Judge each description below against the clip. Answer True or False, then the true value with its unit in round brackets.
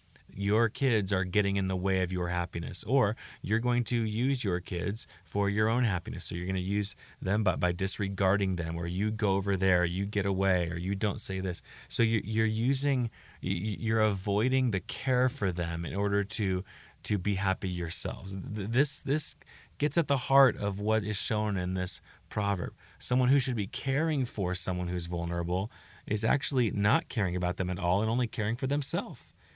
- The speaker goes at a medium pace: True (195 wpm)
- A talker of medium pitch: False (100 Hz)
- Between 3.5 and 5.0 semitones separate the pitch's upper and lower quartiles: True (3.9 semitones)